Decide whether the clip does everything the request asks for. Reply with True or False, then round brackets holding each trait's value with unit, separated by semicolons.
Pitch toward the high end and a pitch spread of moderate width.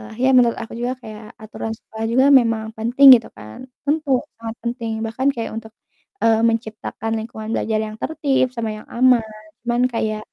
False (230 Hz; 2.0 semitones)